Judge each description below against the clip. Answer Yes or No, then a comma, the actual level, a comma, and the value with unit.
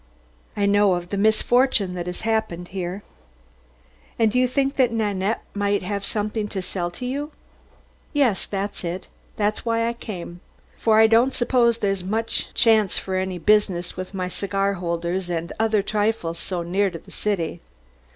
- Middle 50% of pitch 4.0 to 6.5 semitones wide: No, average, 3.5 semitones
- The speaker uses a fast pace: No, average, 165 wpm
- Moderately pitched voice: No, high, 200 Hz